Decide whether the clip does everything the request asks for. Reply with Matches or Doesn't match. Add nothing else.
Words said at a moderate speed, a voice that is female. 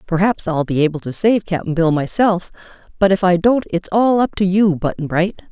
Doesn't match